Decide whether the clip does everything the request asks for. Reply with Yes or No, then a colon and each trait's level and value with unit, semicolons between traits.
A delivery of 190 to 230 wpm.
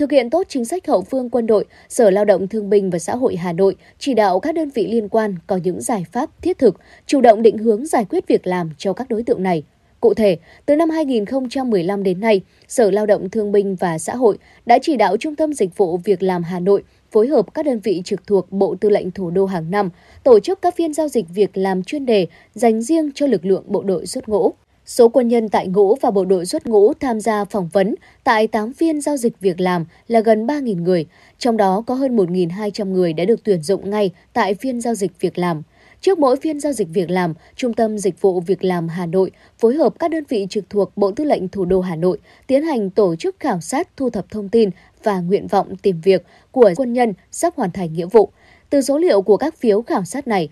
No: average, 245 wpm